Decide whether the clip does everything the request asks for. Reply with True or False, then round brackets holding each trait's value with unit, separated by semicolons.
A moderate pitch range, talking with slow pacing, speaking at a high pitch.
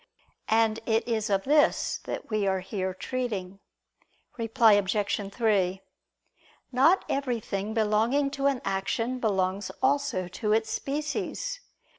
True (4.4 semitones; 120 wpm; 220 Hz)